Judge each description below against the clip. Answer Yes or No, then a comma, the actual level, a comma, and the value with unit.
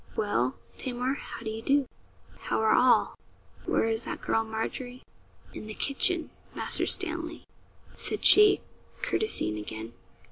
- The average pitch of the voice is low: No, high, 245 Hz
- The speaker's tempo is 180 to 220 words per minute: No, slow, 135 wpm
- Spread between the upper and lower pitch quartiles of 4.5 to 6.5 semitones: Yes, average, 4.8 semitones